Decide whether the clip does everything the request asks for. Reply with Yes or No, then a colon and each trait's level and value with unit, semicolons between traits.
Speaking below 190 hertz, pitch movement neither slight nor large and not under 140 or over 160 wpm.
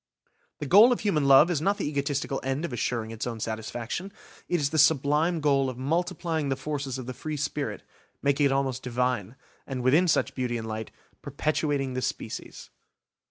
No: medium, 140 Hz; average, 3.4 semitones; average, 180 wpm